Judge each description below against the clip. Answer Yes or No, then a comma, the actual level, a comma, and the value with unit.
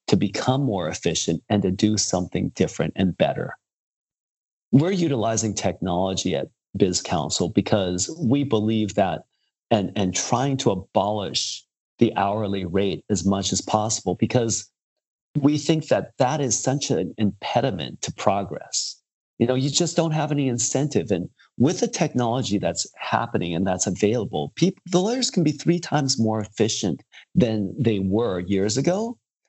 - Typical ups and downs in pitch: No, wide, 6.1 semitones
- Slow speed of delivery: No, average, 155 wpm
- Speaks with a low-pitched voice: Yes, low, 110 Hz